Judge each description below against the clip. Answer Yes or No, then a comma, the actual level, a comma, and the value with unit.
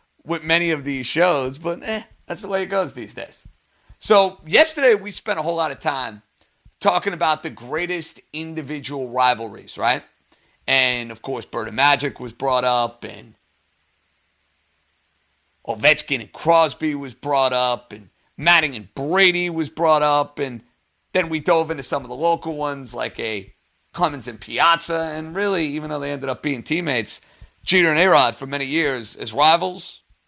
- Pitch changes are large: Yes, wide, 5.7 semitones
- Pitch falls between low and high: Yes, medium, 145 Hz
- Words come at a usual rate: Yes, average, 170 wpm